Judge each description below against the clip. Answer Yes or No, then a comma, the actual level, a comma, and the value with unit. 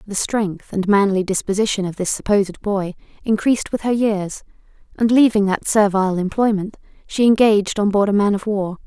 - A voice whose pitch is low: No, high, 205 Hz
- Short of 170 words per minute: No, average, 175 wpm